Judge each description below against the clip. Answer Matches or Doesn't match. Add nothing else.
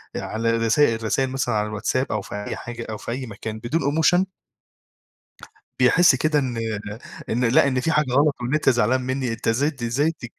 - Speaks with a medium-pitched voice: Doesn't match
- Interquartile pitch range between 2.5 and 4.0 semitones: Matches